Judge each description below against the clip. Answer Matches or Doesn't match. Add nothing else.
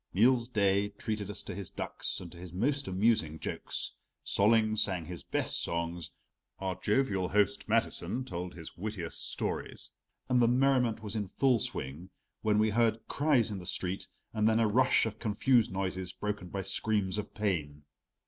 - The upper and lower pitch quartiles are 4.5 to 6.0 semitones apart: Doesn't match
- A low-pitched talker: Matches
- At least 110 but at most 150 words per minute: Doesn't match